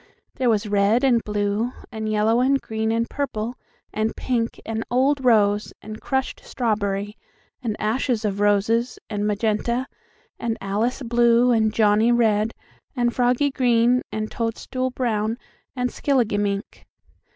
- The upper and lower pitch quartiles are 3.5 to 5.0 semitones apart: No, narrow, 2.6 semitones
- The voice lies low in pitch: No, high, 225 Hz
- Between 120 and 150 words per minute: Yes, slow, 135 wpm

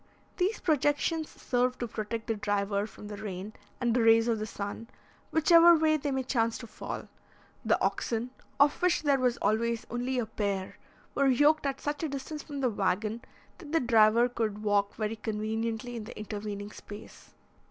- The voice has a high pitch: Yes, high, 230 Hz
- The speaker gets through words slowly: No, average, 180 wpm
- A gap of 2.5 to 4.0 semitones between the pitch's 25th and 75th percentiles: No, average, 4.6 semitones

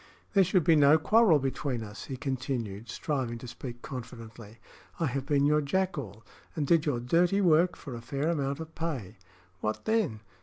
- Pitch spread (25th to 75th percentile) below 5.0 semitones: No, average, 5.3 semitones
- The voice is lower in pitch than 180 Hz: Yes, medium, 140 Hz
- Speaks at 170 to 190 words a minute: Yes, average, 180 wpm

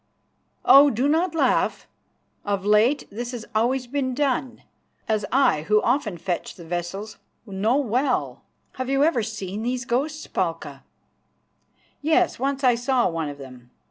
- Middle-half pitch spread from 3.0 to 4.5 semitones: No, average, 5.1 semitones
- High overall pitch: Yes, high, 240 Hz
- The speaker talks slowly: No, average, 145 wpm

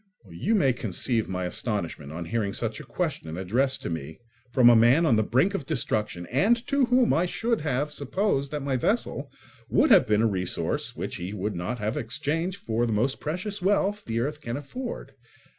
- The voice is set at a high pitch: No, low, 125 Hz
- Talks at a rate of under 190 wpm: No, average, 195 wpm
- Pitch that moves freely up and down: Yes, wide, 7.3 semitones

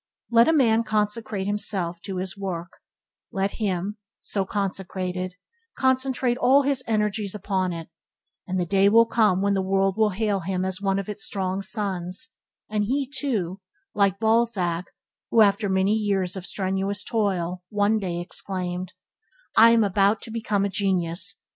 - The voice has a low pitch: No, high, 200 Hz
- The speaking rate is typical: Yes, average, 160 wpm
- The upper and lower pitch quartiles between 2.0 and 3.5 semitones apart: Yes, narrow, 2.6 semitones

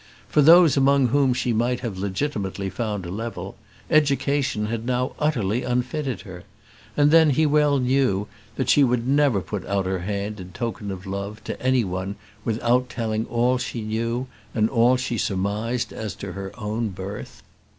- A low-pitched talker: Yes, low, 115 Hz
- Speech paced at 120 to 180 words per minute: Yes, average, 170 wpm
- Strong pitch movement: No, average, 4.4 semitones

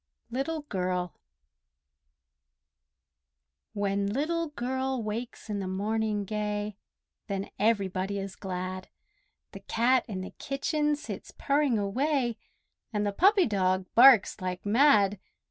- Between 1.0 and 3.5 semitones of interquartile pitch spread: No, average, 5.1 semitones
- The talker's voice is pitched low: No, high, 210 Hz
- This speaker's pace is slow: Yes, slow, 110 wpm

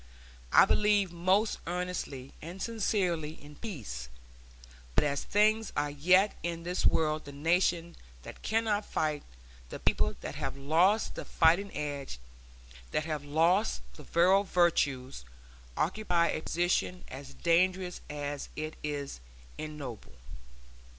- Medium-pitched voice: Yes, medium, 165 Hz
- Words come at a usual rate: No, slow, 125 wpm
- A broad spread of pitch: No, average, 4.1 semitones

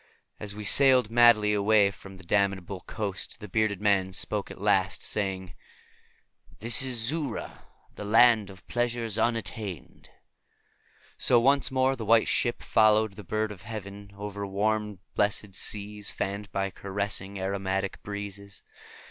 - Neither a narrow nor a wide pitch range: No, narrow, 2.0 semitones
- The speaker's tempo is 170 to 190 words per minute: No, average, 140 wpm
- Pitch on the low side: Yes, low, 105 Hz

